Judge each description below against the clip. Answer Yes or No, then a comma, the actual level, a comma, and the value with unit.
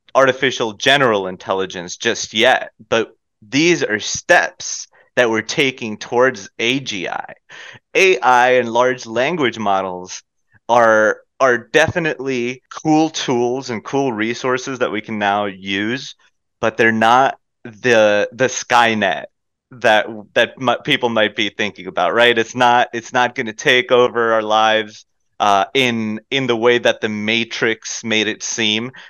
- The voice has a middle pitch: No, low, 115 Hz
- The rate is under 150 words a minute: Yes, average, 140 wpm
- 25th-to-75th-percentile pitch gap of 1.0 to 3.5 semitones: Yes, average, 2.7 semitones